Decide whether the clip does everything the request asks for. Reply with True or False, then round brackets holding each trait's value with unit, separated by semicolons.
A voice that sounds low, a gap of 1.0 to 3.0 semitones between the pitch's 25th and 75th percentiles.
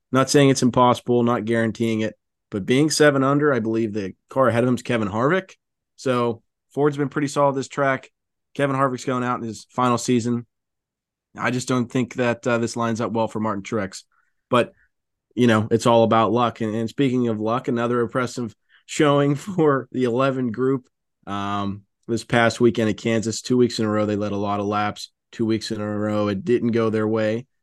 True (120 Hz; 2.6 semitones)